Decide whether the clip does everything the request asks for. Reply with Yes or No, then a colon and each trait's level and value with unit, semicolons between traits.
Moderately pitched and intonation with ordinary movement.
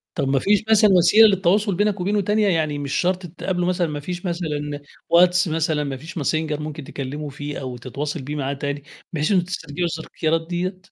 Yes: medium, 165 Hz; average, 3.9 semitones